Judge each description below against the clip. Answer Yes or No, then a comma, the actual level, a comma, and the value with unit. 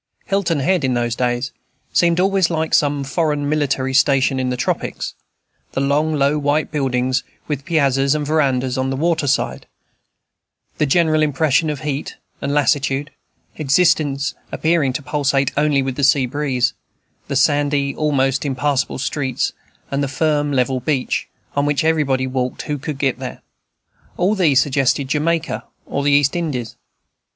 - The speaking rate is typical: Yes, average, 155 wpm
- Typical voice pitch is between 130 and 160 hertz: Yes, medium, 140 Hz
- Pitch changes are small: Yes, narrow, 2.3 semitones